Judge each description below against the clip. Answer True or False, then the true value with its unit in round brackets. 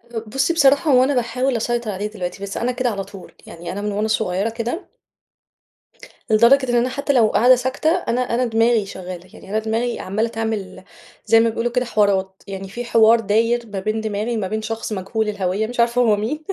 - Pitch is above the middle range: True (225 Hz)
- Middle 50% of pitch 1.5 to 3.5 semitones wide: True (3.0 semitones)